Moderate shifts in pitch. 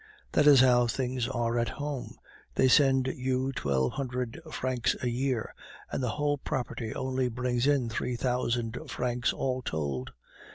No: narrow, 1.8 semitones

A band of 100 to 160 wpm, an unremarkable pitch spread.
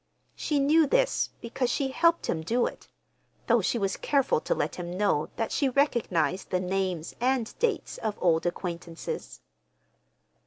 No: average, 150 wpm; wide, 7.6 semitones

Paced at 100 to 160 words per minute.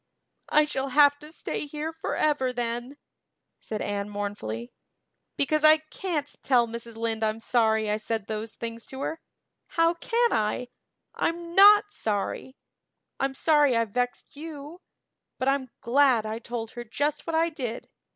Yes: average, 150 wpm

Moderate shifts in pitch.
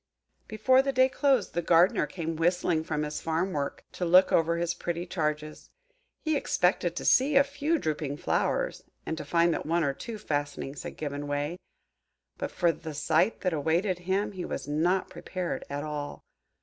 Yes: average, 3.7 semitones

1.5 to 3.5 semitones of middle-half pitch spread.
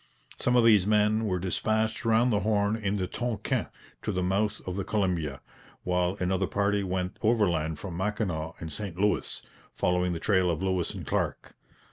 Yes: average, 2.9 semitones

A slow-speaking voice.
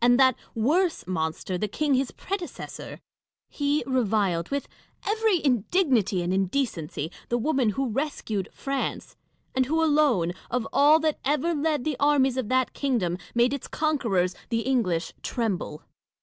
No: average, 155 wpm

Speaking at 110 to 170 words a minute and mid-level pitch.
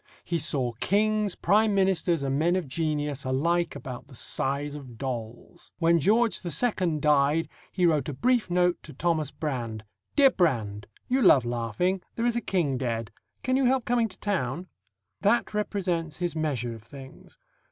Yes: average, 165 wpm; medium, 160 Hz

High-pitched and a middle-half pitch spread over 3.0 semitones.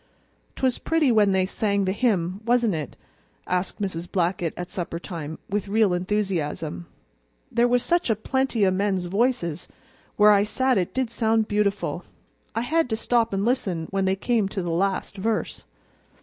Yes: high, 200 Hz; average, 4.1 semitones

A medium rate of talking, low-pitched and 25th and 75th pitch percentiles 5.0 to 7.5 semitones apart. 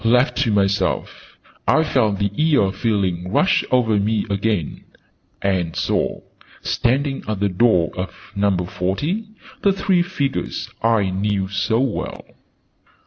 No: slow, 130 wpm; low, 105 Hz; wide, 5.5 semitones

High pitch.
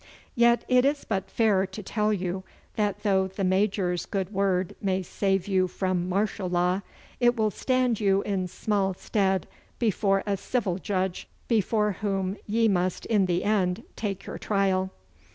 Yes: high, 195 Hz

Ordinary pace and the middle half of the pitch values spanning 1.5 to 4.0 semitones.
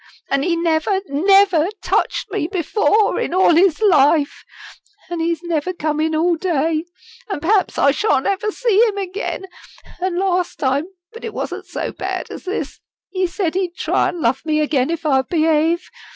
Yes: average, 175 wpm; average, 3.7 semitones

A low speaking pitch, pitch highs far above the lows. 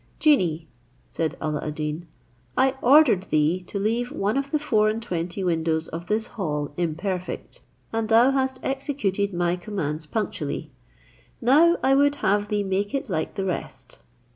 No: high, 200 Hz; wide, 6.7 semitones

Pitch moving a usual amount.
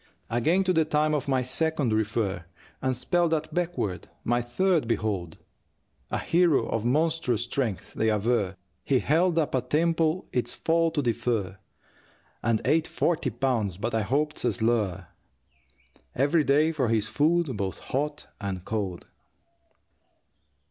No: wide, 6.4 semitones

